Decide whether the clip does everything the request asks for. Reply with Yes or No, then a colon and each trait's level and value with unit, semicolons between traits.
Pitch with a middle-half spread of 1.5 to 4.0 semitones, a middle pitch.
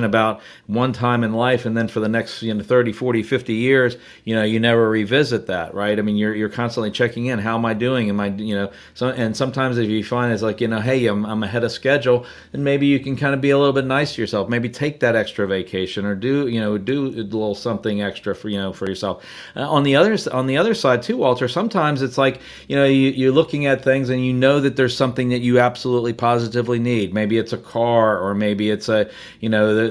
No: average, 3.3 semitones; low, 120 Hz